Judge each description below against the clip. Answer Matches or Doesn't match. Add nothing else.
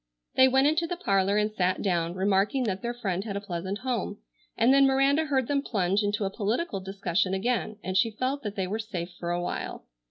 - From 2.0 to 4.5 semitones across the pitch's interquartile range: Doesn't match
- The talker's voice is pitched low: Doesn't match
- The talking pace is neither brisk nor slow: Doesn't match